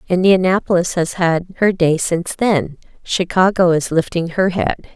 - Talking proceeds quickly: No, average, 145 wpm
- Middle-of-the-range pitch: Yes, medium, 175 Hz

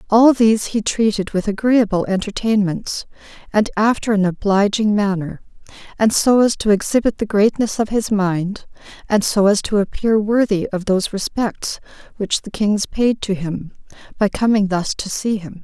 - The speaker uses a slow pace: No, average, 165 wpm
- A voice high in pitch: Yes, high, 205 Hz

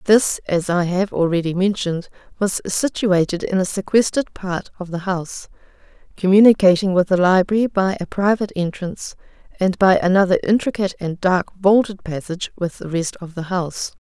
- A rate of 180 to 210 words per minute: No, average, 160 wpm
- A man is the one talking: No, female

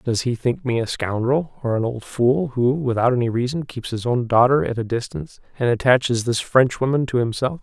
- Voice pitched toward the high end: No, low, 125 Hz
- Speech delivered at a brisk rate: Yes, fast, 215 wpm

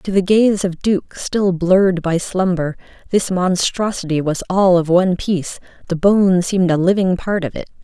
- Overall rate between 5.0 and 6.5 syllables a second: No, 4.7 syllables/s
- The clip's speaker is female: Yes, female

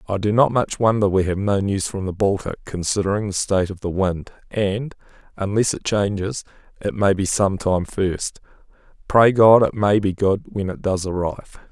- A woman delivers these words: No, male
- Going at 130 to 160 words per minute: No, average, 195 wpm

